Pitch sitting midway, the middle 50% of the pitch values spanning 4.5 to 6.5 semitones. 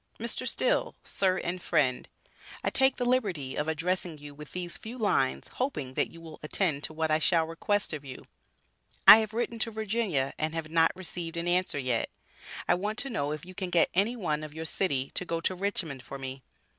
Yes: medium, 170 Hz; average, 4.9 semitones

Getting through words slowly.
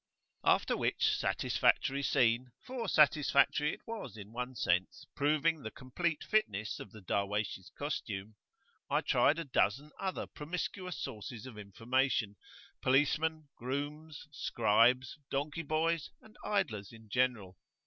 Yes: slow, 125 wpm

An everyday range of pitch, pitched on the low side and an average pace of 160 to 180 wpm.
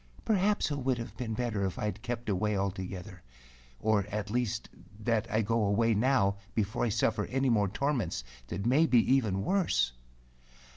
Yes: average, 3.7 semitones; low, 110 Hz; average, 175 wpm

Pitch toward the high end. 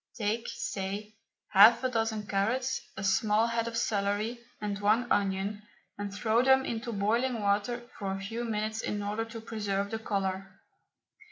Yes: high, 215 Hz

